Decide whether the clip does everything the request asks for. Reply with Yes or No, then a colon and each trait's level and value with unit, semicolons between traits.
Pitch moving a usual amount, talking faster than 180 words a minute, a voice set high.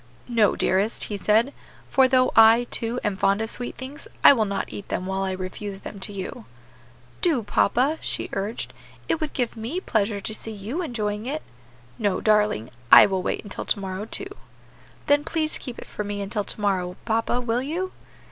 Yes: average, 4.1 semitones; average, 195 wpm; high, 220 Hz